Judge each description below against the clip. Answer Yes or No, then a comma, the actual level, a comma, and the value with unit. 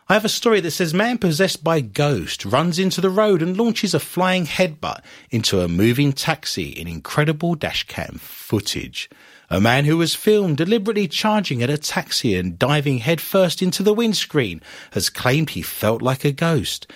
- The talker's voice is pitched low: No, medium, 160 Hz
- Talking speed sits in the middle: Yes, average, 175 wpm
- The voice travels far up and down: Yes, wide, 6.6 semitones